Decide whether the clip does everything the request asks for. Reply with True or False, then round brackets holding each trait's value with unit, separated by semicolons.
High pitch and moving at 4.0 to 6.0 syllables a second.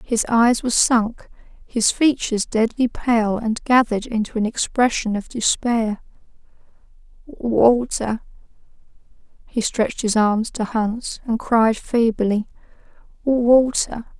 False (230 Hz; 3.8 syllables/s)